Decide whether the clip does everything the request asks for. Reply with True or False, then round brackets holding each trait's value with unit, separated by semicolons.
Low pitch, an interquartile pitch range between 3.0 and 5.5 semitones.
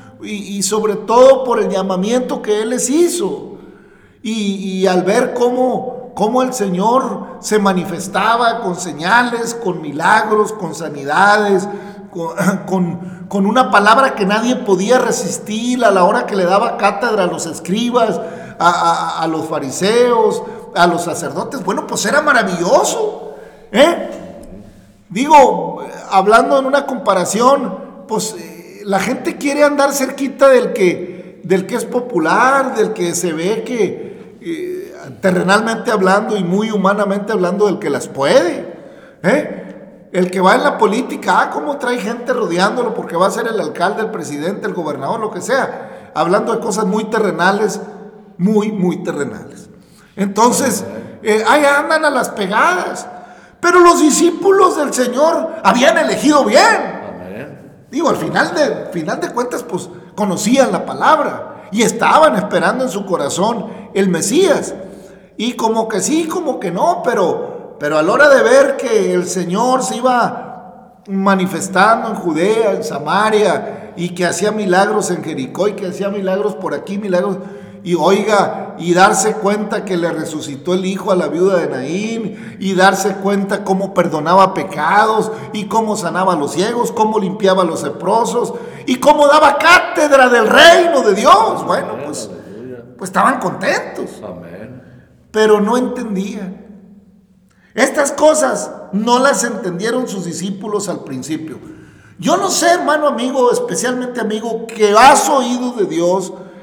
False (210 Hz; 4.8 semitones)